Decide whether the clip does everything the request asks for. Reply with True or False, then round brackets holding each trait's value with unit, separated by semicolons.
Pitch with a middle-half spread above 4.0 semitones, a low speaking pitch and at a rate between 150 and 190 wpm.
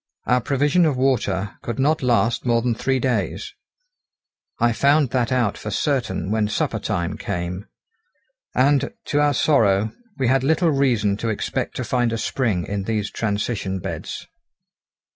True (4.6 semitones; 120 Hz; 155 wpm)